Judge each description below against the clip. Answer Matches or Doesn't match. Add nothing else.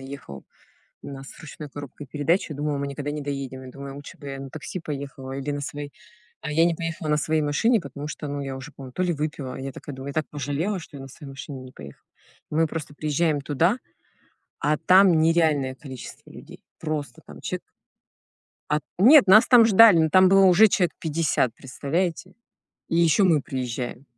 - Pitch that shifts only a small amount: Doesn't match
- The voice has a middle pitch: Matches